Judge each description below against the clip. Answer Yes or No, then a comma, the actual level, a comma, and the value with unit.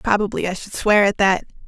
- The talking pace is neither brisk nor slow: No, fast, 215 wpm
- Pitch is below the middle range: No, high, 200 Hz